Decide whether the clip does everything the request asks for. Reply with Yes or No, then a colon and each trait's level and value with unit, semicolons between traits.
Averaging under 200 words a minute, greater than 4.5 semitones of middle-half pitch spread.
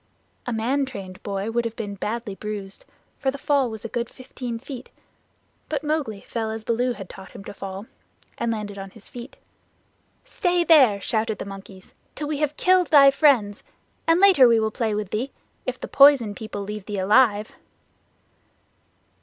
Yes: average, 180 wpm; average, 4.9 semitones